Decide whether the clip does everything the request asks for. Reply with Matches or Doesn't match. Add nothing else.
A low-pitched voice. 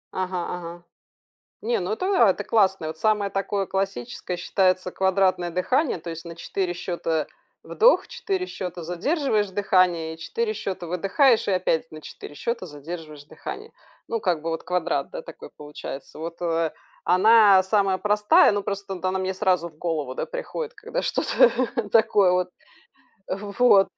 Doesn't match